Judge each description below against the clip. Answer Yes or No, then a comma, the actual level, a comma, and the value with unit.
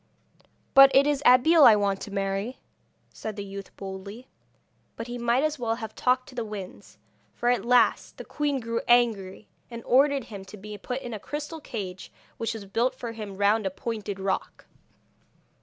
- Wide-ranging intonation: No, average, 4.0 semitones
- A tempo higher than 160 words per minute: Yes, average, 185 wpm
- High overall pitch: Yes, high, 230 Hz